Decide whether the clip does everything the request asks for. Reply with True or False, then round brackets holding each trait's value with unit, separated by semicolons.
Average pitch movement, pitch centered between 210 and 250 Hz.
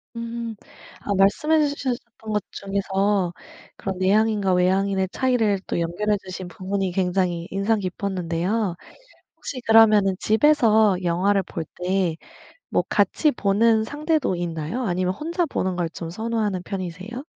False (3.4 semitones; 200 Hz)